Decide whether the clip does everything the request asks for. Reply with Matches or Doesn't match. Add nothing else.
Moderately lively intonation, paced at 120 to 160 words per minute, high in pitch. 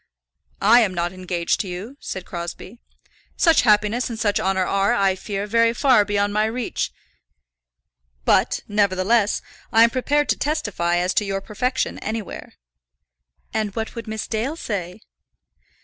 Matches